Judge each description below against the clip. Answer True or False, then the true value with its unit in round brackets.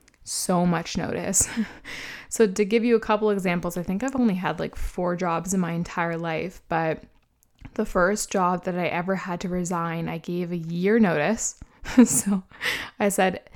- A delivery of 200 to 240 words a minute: False (175 wpm)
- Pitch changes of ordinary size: True (3.3 semitones)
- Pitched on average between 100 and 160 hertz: False (180 Hz)